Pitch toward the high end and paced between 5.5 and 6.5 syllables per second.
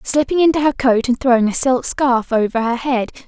No: very high, 255 Hz; 5.3 syllables/s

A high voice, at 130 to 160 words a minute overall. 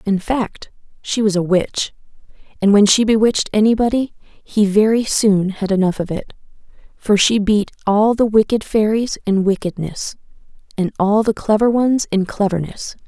Yes: high, 210 Hz; average, 155 wpm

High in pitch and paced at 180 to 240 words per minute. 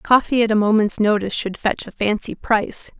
Yes: high, 215 Hz; average, 200 wpm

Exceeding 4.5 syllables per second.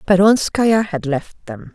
No: 3.8 syllables/s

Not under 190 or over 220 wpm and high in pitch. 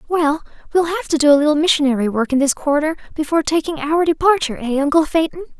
Yes: fast, 205 wpm; very high, 305 Hz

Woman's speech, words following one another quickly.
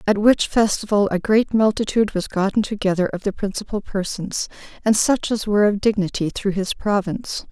No: female; average, 175 wpm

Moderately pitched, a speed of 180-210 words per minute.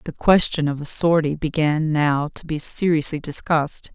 No: medium, 155 Hz; average, 165 wpm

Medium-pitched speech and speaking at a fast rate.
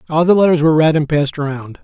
Yes: medium, 155 Hz; fast, 260 wpm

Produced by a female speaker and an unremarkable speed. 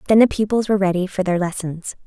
No: female; fast, 235 wpm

